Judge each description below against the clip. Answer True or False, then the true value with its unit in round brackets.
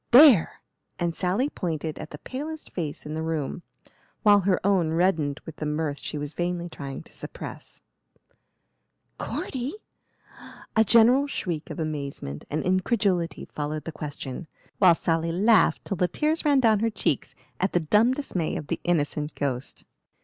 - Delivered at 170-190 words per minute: False (155 wpm)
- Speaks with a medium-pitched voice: True (175 Hz)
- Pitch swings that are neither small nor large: False (5.8 semitones)